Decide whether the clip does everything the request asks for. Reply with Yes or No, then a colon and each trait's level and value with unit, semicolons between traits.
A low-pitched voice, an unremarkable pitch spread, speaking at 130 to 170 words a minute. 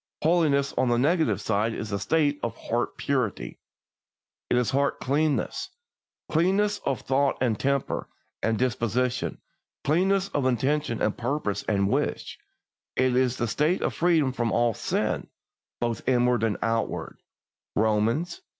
Yes: low, 130 Hz; average, 4.6 semitones; average, 140 wpm